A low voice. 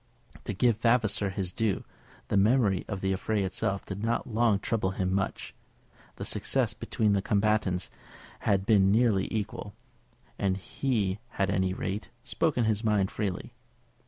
Yes: low, 100 Hz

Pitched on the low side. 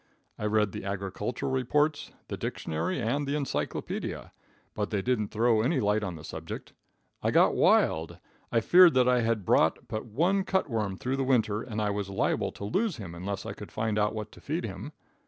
Yes: low, 110 Hz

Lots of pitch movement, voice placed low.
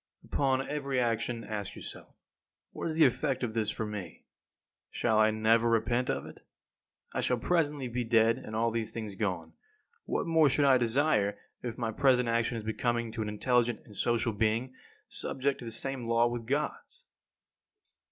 No: average, 2.9 semitones; low, 115 Hz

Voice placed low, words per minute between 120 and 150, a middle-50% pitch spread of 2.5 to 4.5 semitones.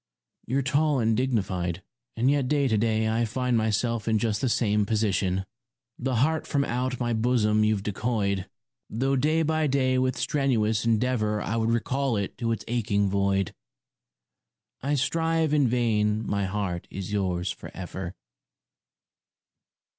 Yes: low, 115 Hz; average, 145 wpm; average, 3.8 semitones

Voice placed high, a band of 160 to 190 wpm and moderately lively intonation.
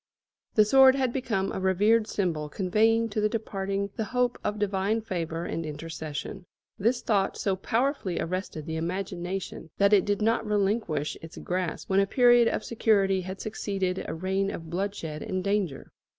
Yes: high, 195 Hz; average, 165 wpm; average, 3.3 semitones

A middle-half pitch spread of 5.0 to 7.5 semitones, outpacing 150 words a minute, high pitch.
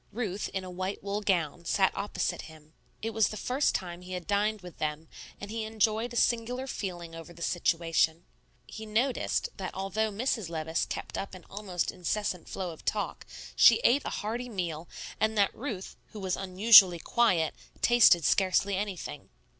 No: average, 3.9 semitones; average, 175 wpm; high, 195 Hz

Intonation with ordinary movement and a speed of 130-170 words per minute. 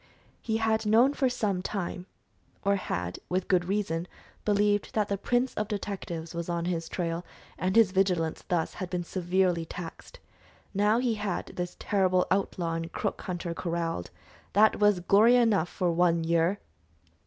Yes: average, 3.4 semitones; average, 160 wpm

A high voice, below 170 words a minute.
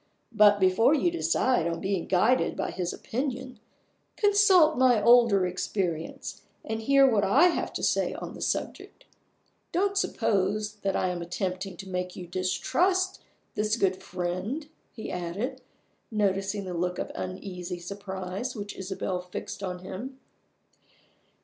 Yes: high, 200 Hz; average, 140 wpm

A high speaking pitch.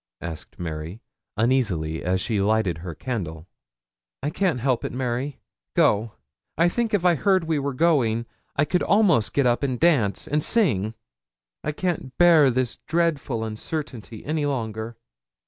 No: low, 130 Hz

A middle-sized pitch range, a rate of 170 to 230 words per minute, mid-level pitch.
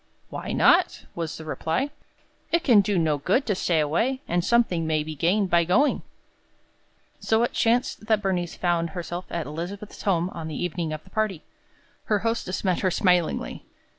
Yes: average, 4.4 semitones; average, 175 wpm; medium, 180 Hz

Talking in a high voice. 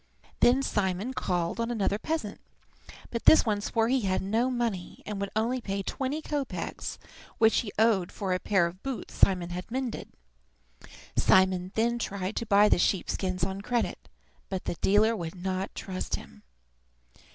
Yes: high, 205 Hz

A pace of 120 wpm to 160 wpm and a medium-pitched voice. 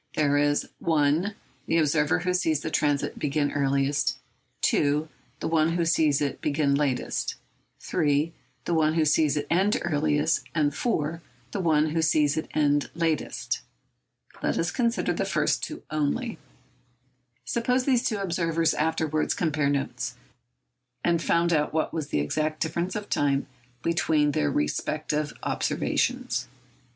Yes: average, 140 wpm; medium, 155 Hz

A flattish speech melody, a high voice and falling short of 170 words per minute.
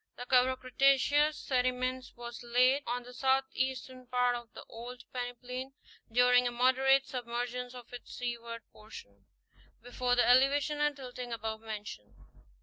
Yes: narrow, 1.3 semitones; very high, 250 Hz; average, 145 wpm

